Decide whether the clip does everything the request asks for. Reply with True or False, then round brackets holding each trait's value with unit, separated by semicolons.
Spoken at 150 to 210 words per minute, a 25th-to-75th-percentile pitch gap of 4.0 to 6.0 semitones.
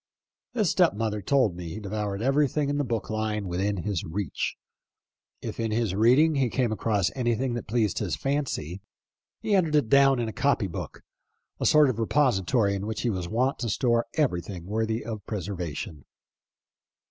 True (180 wpm; 4.9 semitones)